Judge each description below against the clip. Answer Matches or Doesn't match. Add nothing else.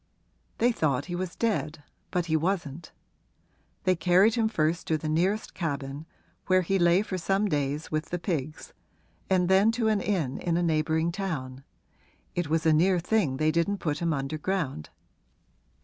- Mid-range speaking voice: Matches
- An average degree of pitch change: Matches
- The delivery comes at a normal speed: Matches